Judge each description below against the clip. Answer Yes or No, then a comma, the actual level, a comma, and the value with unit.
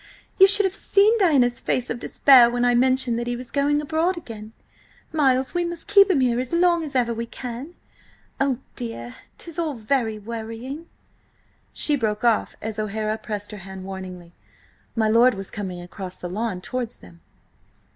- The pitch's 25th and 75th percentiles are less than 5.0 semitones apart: No, average, 5.3 semitones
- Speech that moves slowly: No, average, 175 wpm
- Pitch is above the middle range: Yes, high, 240 Hz